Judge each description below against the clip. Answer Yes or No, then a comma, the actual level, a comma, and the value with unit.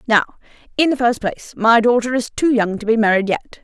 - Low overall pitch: No, high, 230 Hz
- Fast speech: Yes, fast, 230 wpm